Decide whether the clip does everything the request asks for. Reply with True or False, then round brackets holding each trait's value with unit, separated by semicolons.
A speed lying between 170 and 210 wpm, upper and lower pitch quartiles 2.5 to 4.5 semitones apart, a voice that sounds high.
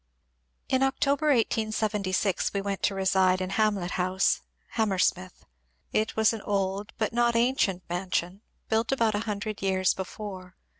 False (145 wpm; 2.8 semitones; 205 Hz)